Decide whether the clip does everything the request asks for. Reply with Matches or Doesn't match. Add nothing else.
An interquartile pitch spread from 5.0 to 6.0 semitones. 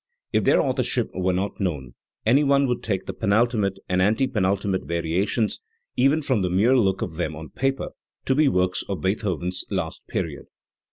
Matches